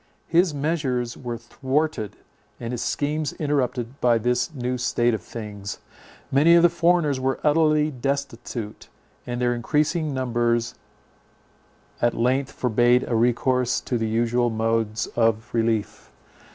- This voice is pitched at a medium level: No, low, 125 Hz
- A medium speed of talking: No, slow, 130 wpm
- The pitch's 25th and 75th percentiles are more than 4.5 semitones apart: No, average, 3.4 semitones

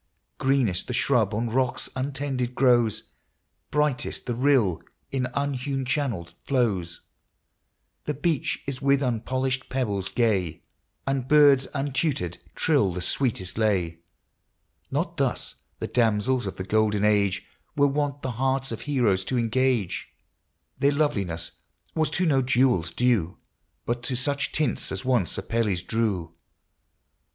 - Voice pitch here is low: Yes, low, 125 Hz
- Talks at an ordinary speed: No, slow, 130 wpm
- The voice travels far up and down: No, average, 4.7 semitones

